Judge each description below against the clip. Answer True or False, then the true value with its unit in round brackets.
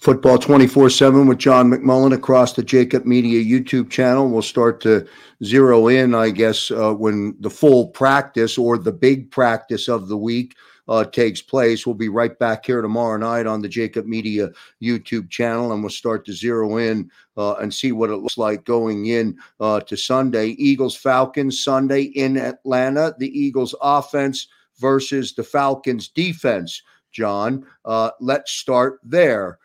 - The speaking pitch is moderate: False (120 Hz)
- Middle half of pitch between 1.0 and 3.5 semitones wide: True (3.0 semitones)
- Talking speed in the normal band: True (165 wpm)